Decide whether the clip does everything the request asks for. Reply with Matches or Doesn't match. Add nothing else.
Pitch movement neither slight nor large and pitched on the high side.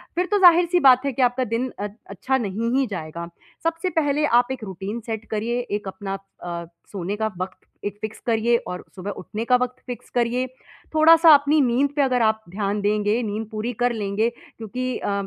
Matches